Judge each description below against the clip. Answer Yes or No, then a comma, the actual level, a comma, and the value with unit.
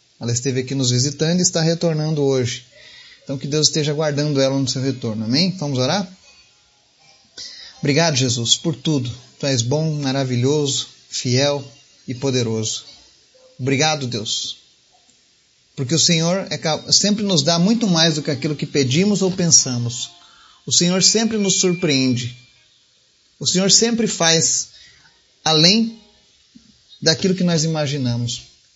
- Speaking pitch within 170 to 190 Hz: No, medium, 145 Hz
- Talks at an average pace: Yes, average, 135 wpm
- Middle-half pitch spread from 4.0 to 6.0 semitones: Yes, average, 4.7 semitones